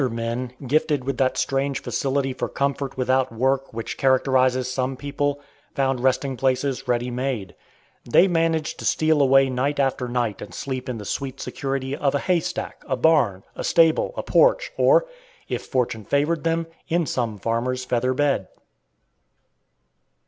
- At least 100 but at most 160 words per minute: Yes, average, 155 wpm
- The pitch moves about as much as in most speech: No, narrow, 2.2 semitones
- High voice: No, low, 135 Hz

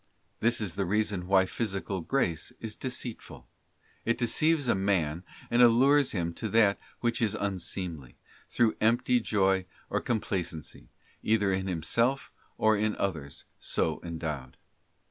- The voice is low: Yes, low, 100 Hz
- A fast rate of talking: No, average, 140 wpm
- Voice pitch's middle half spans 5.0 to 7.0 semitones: No, average, 4.6 semitones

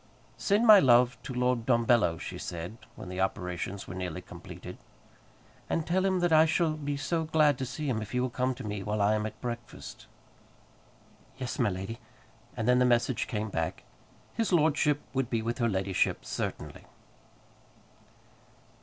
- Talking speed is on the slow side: No, average, 170 wpm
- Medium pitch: No, low, 125 Hz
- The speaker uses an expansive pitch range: Yes, wide, 5.7 semitones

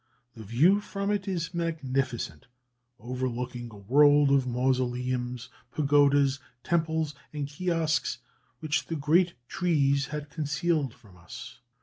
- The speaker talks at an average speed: No, slow, 115 wpm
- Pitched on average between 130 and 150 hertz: Yes, medium, 140 Hz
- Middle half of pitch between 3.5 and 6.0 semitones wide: Yes, average, 4.1 semitones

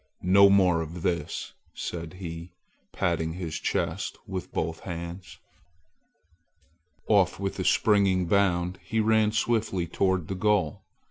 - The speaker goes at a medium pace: No, slow, 125 wpm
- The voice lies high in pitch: No, very low, 90 Hz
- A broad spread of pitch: No, narrow, 2.6 semitones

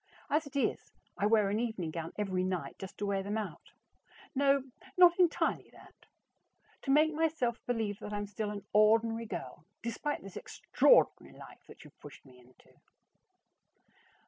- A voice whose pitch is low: No, high, 215 Hz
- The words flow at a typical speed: Yes, average, 165 wpm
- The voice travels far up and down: Yes, wide, 5.8 semitones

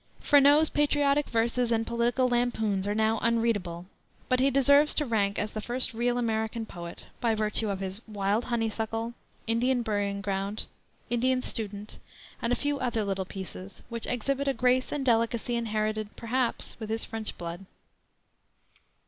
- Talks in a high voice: Yes, high, 230 Hz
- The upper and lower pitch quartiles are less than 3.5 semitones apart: Yes, average, 2.8 semitones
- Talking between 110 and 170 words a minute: Yes, average, 155 wpm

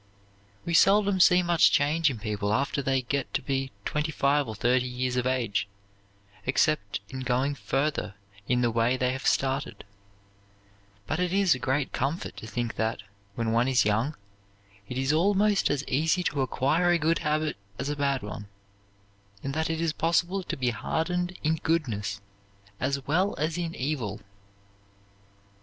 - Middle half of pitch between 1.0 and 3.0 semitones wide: No, average, 4.4 semitones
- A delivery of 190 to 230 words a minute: No, average, 165 wpm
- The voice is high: No, medium, 140 Hz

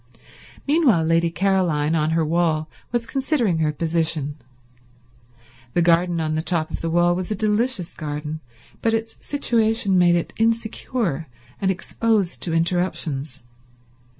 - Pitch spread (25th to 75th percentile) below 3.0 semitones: No, wide, 5.4 semitones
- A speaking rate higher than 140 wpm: No, slow, 135 wpm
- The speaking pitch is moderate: Yes, medium, 175 Hz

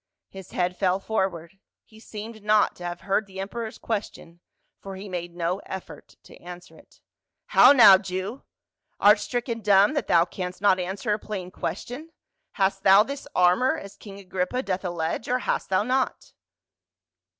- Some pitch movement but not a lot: Yes, average, 3.1 semitones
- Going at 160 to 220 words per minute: Yes, average, 170 wpm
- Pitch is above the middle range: Yes, high, 195 Hz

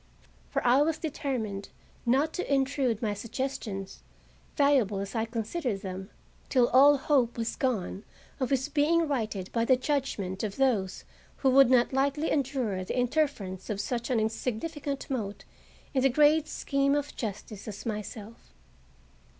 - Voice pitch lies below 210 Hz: No, very high, 250 Hz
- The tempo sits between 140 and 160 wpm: Yes, average, 150 wpm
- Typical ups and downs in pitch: Yes, average, 4.8 semitones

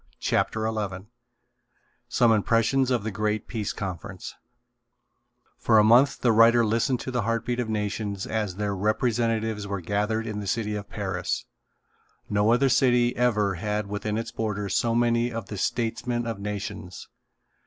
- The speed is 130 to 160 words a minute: Yes, average, 155 wpm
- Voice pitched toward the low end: Yes, low, 110 Hz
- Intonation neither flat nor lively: No, narrow, 2.3 semitones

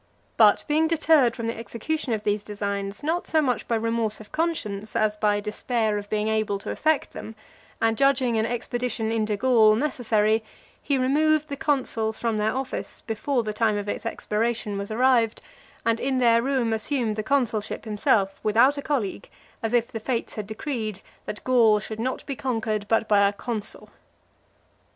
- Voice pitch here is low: No, high, 225 Hz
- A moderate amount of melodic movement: Yes, average, 3.3 semitones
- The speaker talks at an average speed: Yes, average, 180 wpm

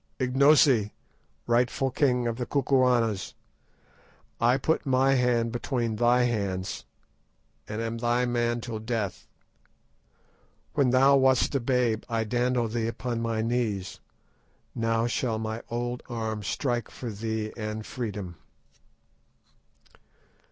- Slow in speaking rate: Yes, slow, 115 wpm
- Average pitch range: No, narrow, 2.1 semitones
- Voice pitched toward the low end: Yes, low, 120 Hz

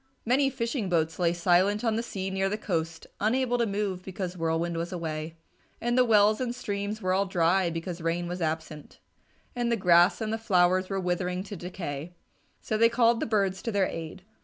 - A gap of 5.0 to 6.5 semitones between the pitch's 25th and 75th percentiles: No, average, 4.1 semitones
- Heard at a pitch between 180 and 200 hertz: Yes, high, 190 Hz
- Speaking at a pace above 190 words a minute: Yes, average, 200 wpm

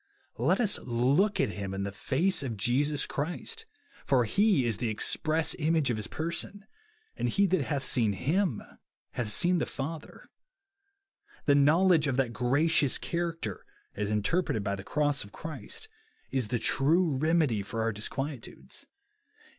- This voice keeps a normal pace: Yes, average, 155 wpm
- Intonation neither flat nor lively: No, wide, 6.4 semitones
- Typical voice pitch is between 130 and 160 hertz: Yes, medium, 140 Hz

